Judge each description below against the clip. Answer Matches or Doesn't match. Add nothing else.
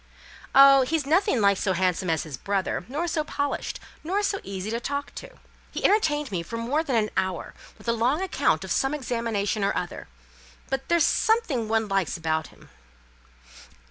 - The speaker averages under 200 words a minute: Matches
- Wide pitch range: Matches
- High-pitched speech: Matches